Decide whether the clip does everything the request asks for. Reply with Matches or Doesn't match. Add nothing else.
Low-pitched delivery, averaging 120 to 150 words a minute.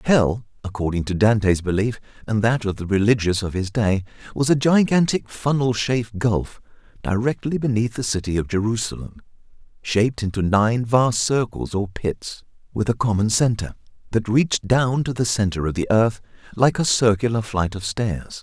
Doesn't match